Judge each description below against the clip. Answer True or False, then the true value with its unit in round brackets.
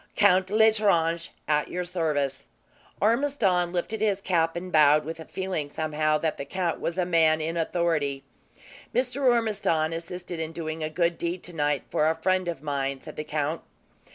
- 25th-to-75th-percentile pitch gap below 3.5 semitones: True (3.1 semitones)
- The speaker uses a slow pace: False (170 wpm)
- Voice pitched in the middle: True (165 Hz)